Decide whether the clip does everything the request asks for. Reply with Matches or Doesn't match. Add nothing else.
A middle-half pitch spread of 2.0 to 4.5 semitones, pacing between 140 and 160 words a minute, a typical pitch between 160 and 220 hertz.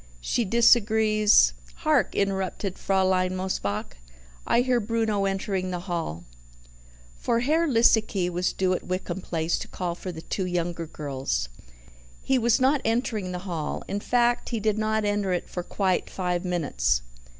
Matches